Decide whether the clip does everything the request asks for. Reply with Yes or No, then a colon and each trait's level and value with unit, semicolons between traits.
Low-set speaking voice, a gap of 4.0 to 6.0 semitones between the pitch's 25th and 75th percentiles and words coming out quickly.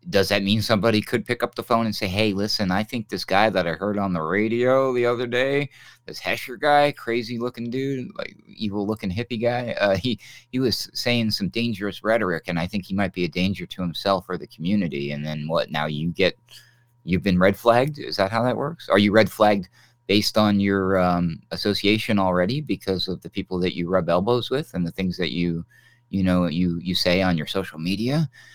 Yes: low, 105 Hz; average, 4.6 semitones; fast, 220 wpm